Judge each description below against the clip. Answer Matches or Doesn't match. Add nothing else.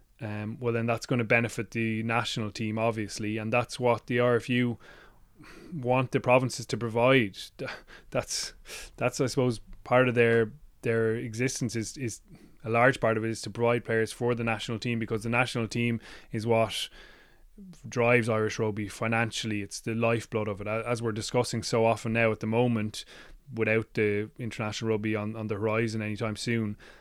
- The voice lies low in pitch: Matches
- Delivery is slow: Doesn't match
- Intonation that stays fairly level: Matches